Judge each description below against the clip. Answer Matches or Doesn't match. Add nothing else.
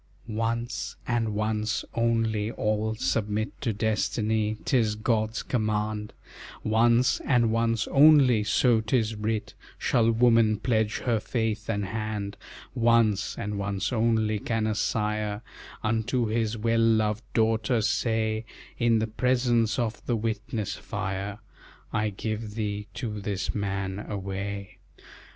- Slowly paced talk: Matches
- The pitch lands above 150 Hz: Doesn't match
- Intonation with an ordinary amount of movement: Doesn't match